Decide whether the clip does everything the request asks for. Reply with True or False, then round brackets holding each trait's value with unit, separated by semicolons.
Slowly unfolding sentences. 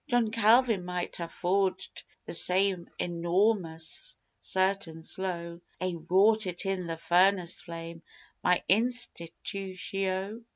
True (110 wpm)